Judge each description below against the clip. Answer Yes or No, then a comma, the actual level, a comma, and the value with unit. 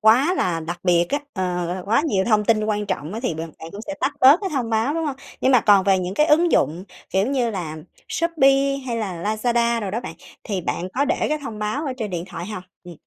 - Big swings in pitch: Yes, wide, 6.4 semitones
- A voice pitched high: Yes, high, 215 Hz